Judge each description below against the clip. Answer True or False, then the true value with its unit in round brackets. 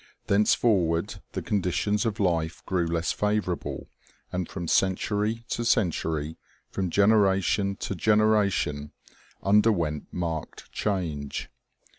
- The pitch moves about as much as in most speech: True (3.9 semitones)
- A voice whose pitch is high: False (95 Hz)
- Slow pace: True (105 wpm)